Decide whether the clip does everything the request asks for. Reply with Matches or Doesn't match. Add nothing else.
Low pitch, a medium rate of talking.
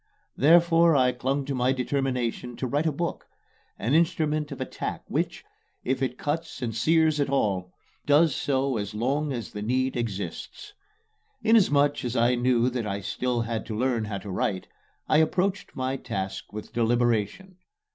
Matches